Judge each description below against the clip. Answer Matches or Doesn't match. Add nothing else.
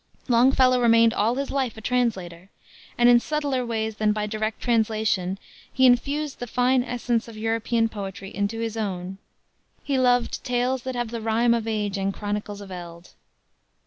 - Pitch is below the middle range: Doesn't match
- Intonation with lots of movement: Doesn't match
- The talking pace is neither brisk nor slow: Matches